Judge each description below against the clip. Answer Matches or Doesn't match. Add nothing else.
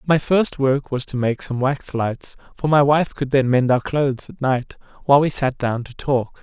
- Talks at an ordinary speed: Doesn't match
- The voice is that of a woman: Doesn't match